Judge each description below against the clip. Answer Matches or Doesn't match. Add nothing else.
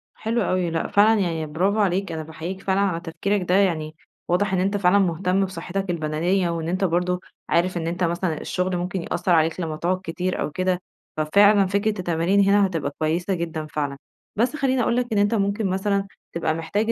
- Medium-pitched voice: Matches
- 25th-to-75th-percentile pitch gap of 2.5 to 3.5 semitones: Matches